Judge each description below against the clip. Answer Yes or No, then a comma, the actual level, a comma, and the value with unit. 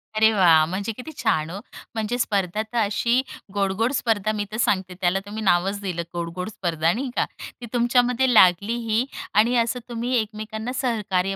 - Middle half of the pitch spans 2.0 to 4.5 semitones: Yes, average, 3.8 semitones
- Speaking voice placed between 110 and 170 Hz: No, high, 215 Hz